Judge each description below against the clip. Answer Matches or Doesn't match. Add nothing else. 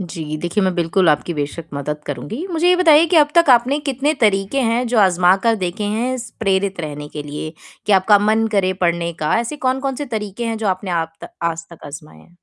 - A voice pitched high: Matches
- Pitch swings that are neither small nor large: Doesn't match